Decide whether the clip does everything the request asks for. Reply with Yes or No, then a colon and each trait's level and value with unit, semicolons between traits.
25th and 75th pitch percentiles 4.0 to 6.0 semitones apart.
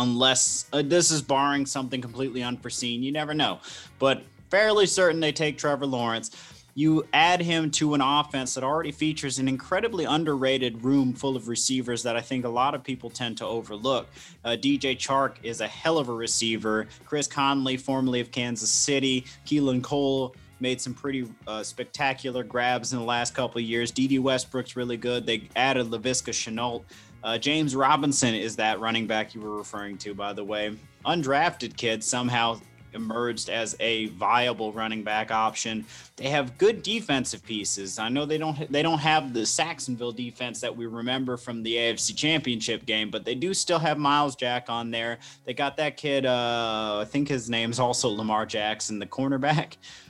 No: average, 3.4 semitones